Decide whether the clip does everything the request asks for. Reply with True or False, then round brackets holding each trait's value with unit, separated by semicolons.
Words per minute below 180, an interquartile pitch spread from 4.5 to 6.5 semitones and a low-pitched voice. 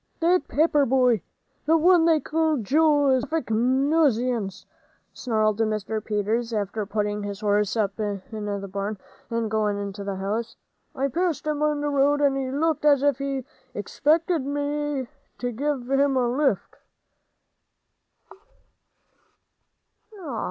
False (140 wpm; 5.5 semitones; 255 Hz)